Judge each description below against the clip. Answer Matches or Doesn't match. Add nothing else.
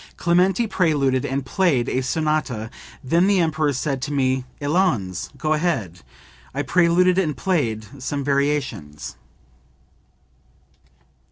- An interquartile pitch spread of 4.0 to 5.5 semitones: Matches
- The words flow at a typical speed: Doesn't match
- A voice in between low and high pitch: Matches